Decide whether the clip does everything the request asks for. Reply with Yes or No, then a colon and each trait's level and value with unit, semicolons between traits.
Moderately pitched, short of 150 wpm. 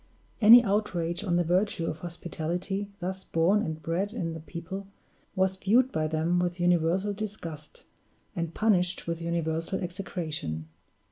Yes: medium, 175 Hz; average, 140 wpm